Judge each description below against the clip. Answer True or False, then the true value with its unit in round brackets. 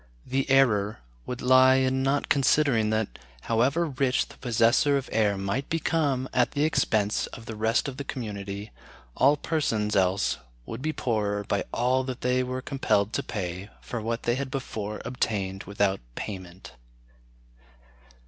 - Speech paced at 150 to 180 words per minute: True (155 wpm)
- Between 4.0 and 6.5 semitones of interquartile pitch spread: True (4.3 semitones)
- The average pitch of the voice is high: False (120 Hz)